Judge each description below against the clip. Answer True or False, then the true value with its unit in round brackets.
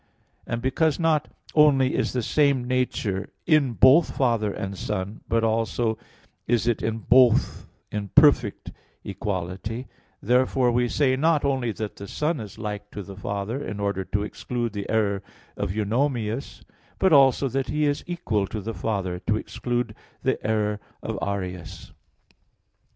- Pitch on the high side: False (115 Hz)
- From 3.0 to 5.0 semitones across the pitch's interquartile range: True (4.4 semitones)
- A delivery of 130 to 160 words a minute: True (150 wpm)